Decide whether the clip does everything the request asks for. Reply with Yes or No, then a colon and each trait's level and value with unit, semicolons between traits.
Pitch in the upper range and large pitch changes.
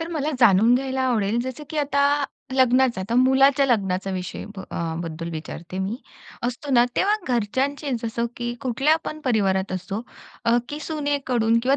Yes: high, 245 Hz; wide, 5.7 semitones